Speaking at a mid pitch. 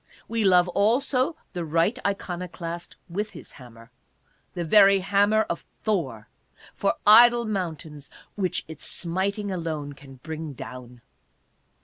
Yes: medium, 180 Hz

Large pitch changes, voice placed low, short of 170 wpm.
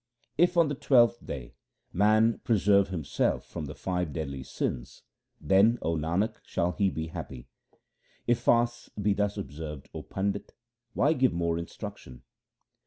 Yes: wide, 6.5 semitones; very low, 95 Hz; average, 150 wpm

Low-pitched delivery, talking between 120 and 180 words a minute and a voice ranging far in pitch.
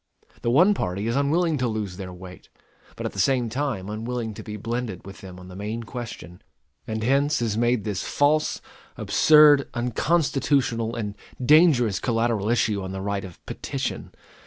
No: low, 115 Hz; average, 170 wpm; average, 5.0 semitones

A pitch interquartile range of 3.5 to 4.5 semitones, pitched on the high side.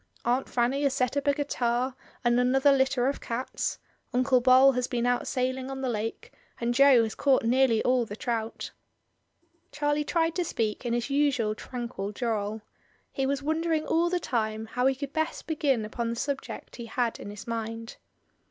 No: average, 3.0 semitones; very high, 255 Hz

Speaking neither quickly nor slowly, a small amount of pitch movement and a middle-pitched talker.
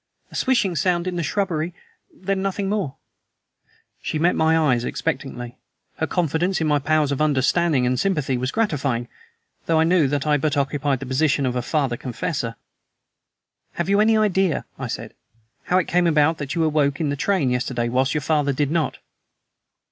No: average, 180 wpm; average, 4.4 semitones; medium, 155 Hz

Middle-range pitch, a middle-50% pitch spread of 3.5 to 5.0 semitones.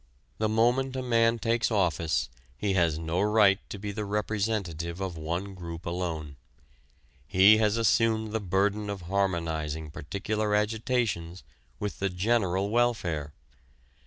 No: low, 100 Hz; average, 4.3 semitones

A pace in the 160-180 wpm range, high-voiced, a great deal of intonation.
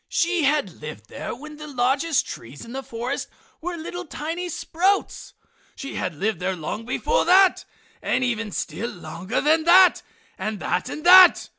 Yes: average, 165 wpm; very high, 270 Hz; wide, 8.2 semitones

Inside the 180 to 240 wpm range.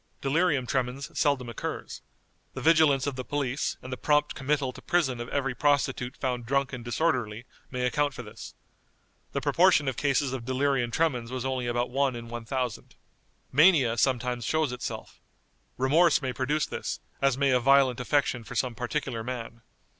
No: average, 170 wpm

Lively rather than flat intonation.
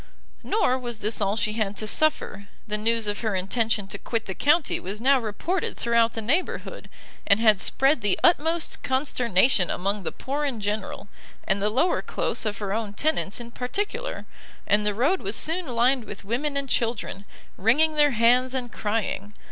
No: average, 4.8 semitones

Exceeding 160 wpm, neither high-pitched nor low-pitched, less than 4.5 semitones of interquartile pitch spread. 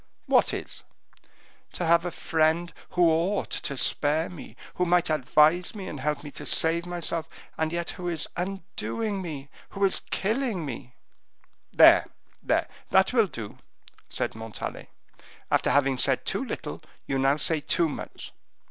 No: average, 150 wpm; medium, 165 Hz; average, 3.3 semitones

